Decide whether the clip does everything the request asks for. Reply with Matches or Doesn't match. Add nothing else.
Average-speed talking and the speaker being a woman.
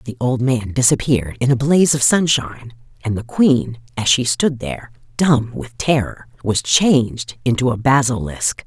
Matches